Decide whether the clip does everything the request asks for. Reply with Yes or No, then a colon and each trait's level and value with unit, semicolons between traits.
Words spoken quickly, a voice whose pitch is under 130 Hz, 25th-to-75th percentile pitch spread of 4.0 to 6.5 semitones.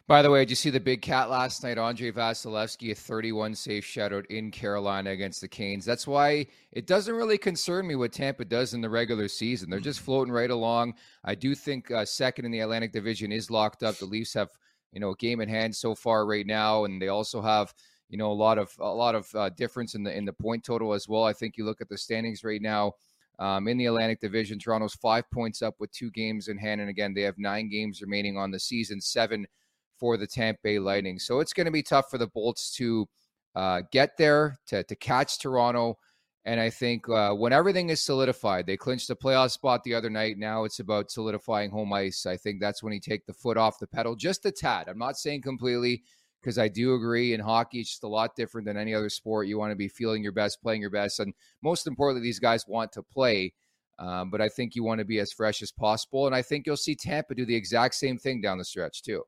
No: fast, 245 wpm; low, 115 Hz; average, 2.8 semitones